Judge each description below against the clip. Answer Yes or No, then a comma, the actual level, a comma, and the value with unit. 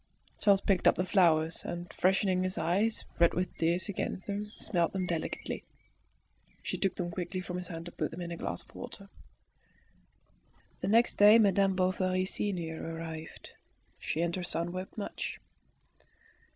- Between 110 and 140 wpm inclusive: No, average, 165 wpm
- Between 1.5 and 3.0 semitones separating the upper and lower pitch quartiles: Yes, narrow, 2.4 semitones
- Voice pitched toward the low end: No, medium, 185 Hz